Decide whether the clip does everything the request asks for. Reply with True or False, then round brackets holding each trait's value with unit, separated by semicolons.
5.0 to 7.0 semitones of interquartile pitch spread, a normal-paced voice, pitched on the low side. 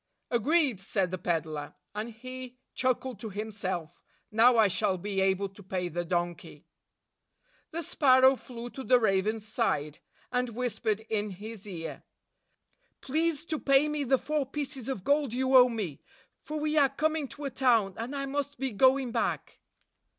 False (5.4 semitones; 165 wpm; 235 Hz)